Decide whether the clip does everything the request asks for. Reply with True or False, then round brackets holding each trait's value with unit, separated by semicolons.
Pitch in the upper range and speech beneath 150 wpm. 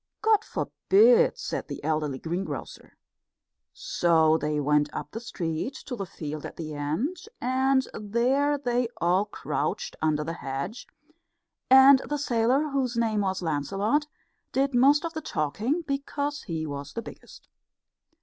True (230 Hz; 140 wpm)